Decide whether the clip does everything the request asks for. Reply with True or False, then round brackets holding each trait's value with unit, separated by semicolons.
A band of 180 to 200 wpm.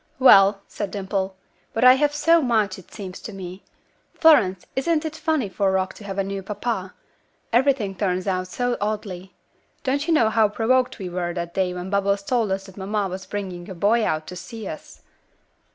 True (195 wpm)